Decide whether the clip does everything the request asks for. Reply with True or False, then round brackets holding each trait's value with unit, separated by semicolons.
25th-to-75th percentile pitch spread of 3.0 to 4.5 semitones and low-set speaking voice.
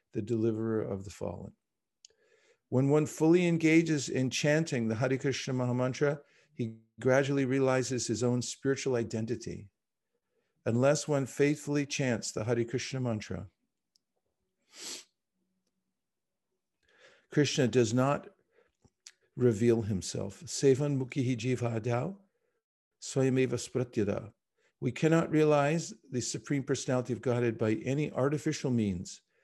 True (3.7 semitones; 130 Hz)